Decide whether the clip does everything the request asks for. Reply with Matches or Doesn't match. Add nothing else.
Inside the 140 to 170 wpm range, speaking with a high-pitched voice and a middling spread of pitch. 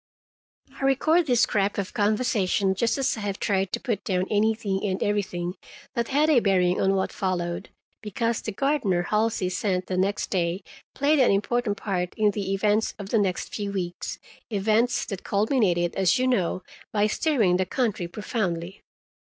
Matches